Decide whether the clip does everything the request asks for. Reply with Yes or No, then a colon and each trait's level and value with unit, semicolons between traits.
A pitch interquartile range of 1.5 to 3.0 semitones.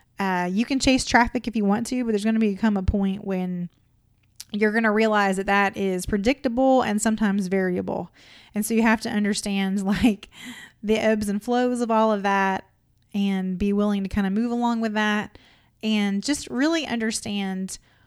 Yes: narrow, 2.6 semitones